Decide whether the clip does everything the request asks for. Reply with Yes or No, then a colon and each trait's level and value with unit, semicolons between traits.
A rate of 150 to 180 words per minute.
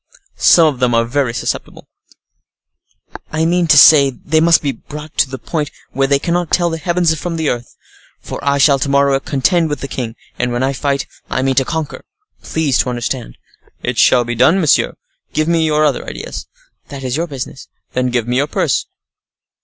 No: average, 195 wpm